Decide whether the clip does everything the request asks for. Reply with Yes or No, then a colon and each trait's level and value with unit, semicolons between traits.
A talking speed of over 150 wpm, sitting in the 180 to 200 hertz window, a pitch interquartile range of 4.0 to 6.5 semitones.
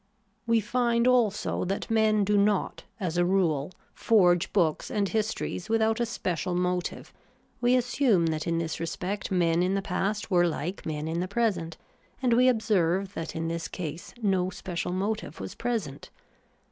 Yes: average, 165 wpm; high, 190 Hz; average, 4.4 semitones